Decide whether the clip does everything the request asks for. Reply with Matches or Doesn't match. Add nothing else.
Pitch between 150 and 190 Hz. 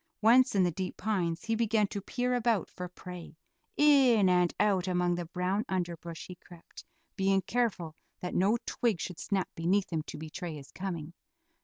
Matches